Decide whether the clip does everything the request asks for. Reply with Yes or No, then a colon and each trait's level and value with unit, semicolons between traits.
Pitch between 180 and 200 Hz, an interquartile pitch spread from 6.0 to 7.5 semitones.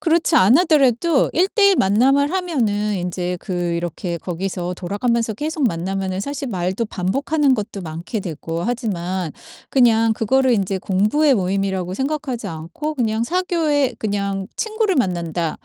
No: high, 215 Hz; wide, 7.0 semitones